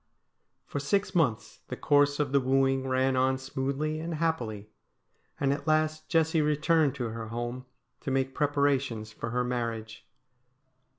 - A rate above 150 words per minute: No, average, 145 wpm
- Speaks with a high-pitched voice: No, low, 135 Hz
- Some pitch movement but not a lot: Yes, average, 3.4 semitones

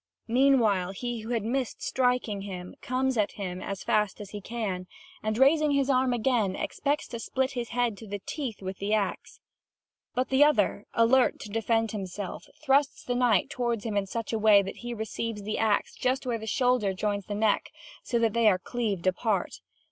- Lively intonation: No, average, 3.5 semitones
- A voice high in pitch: Yes, high, 225 Hz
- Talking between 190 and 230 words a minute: Yes, average, 195 wpm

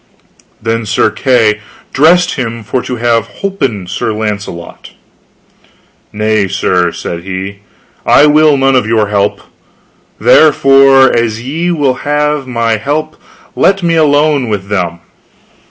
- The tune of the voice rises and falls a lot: Yes, wide, 5.7 semitones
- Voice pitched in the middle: No, low, 120 Hz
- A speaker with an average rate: No, slow, 125 wpm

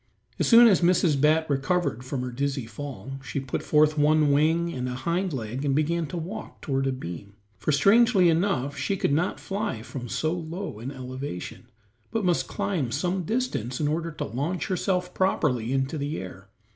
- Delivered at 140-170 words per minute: No, average, 185 wpm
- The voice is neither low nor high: Yes, medium, 150 Hz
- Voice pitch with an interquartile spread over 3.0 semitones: Yes, average, 5.0 semitones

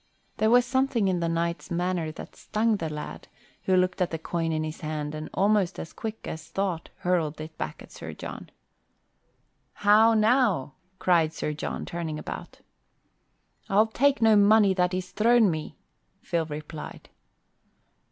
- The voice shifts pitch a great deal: No, average, 5.0 semitones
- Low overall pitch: No, medium, 180 Hz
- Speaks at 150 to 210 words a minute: Yes, average, 160 wpm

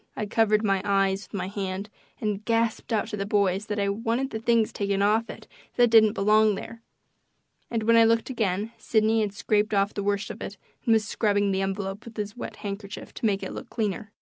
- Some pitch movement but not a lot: No, narrow, 2.1 semitones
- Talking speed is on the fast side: Yes, fast, 220 wpm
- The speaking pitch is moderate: No, high, 210 Hz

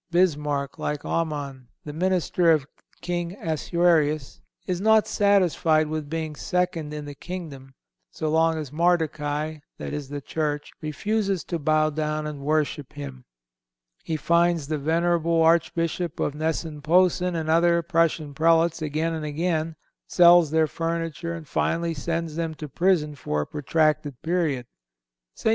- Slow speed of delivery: No, average, 145 wpm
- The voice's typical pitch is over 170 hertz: No, medium, 160 Hz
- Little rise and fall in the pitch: Yes, narrow, 2.2 semitones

